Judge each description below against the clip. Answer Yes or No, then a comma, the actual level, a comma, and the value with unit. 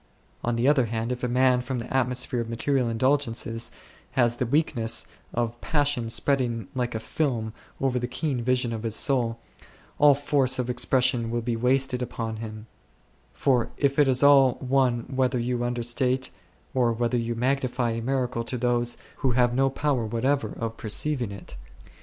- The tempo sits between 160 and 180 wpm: Yes, average, 170 wpm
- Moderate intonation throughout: No, narrow, 2.2 semitones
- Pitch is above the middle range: No, low, 125 Hz